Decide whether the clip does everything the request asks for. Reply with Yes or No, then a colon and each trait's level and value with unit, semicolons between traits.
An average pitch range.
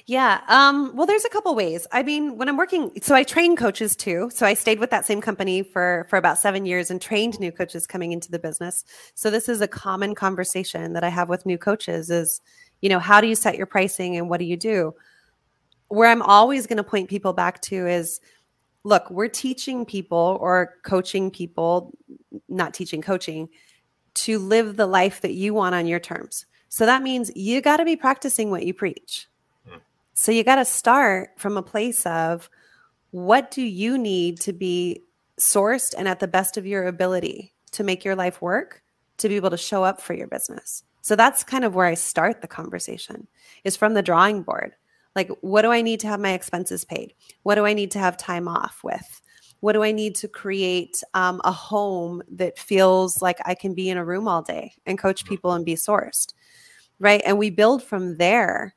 Yes: average, 3.8 semitones